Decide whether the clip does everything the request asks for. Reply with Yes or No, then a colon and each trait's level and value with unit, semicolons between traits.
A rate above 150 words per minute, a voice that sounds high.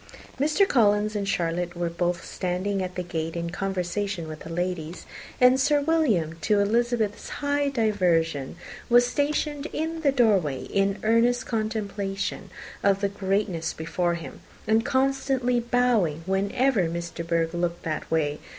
No: average, 145 wpm; high, 200 Hz